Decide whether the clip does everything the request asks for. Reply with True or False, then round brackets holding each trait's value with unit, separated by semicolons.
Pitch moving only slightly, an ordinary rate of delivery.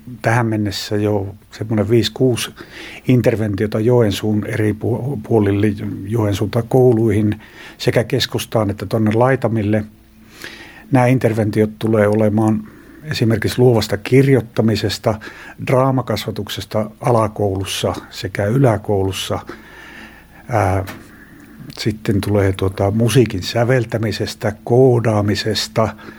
False (2.2 semitones; 75 wpm)